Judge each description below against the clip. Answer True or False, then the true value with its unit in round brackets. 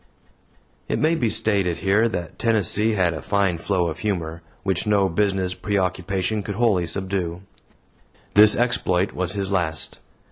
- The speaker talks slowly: False (145 wpm)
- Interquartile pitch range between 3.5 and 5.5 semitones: False (2.9 semitones)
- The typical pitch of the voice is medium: False (95 Hz)